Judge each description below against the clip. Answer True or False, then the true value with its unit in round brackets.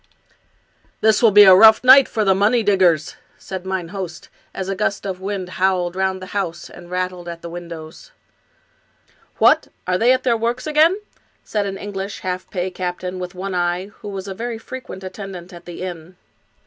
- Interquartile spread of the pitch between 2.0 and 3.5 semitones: True (2.4 semitones)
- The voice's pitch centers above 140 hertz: True (190 Hz)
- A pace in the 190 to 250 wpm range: True (195 wpm)